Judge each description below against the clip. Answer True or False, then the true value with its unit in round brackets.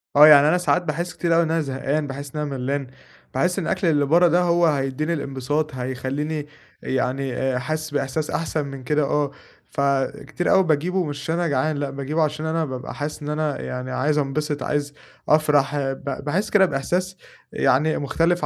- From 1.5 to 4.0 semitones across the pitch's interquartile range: True (2.7 semitones)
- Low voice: False (150 Hz)